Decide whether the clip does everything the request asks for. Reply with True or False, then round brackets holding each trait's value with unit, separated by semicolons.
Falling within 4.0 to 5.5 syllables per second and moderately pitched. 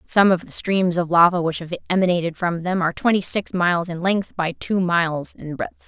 True (5.4 syllables/s; 175 Hz)